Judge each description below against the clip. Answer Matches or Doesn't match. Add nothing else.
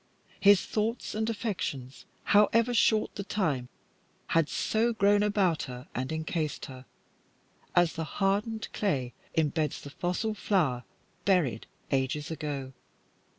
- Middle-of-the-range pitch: Matches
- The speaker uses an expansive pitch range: Matches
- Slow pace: Matches